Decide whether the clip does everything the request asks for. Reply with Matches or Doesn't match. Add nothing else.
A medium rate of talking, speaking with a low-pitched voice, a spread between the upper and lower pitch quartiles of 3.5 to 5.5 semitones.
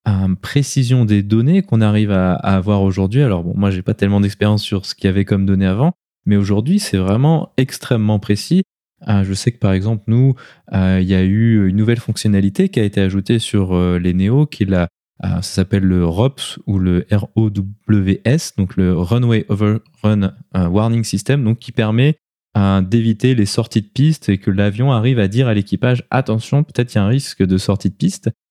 Matches